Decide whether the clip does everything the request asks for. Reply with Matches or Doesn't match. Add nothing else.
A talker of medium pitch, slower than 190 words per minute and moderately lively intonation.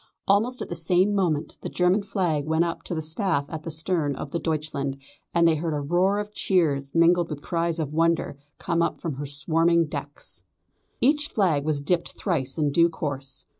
Doesn't match